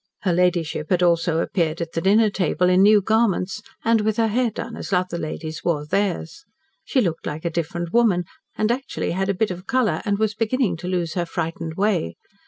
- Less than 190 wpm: No, fast, 205 wpm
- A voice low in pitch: No, medium, 185 Hz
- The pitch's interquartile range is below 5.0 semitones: Yes, average, 4.0 semitones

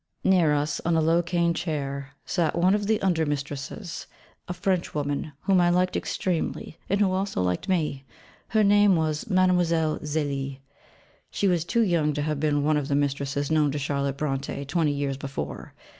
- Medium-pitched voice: Yes, medium, 155 Hz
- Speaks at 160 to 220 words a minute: Yes, average, 175 wpm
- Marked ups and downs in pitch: No, average, 4.0 semitones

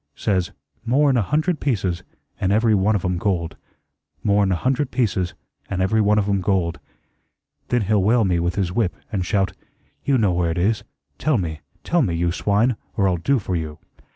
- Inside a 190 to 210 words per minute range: Yes, average, 195 wpm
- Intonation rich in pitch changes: No, average, 4.2 semitones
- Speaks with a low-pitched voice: Yes, low, 100 Hz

